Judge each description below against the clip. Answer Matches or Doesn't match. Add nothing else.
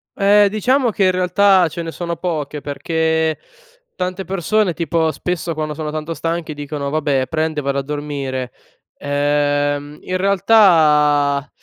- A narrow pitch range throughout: Doesn't match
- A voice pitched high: Doesn't match